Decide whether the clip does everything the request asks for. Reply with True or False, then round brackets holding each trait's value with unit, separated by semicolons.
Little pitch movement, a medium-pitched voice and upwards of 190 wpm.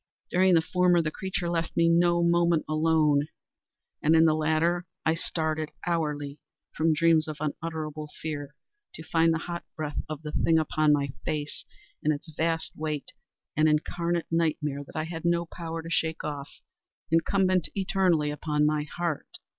False (1.9 semitones; 160 Hz; 155 wpm)